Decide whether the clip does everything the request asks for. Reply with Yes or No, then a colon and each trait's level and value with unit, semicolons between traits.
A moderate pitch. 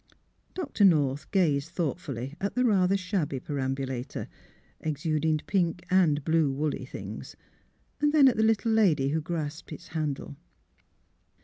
Yes: medium, 160 Hz